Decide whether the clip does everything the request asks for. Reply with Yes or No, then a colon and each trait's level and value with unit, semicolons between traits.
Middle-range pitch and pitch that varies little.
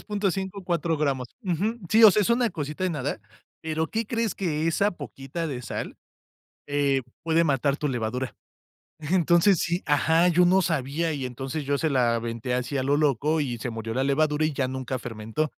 No: medium, 150 Hz; average, 4.6 semitones